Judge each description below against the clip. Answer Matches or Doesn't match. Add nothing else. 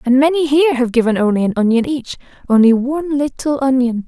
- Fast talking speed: Doesn't match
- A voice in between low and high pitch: Doesn't match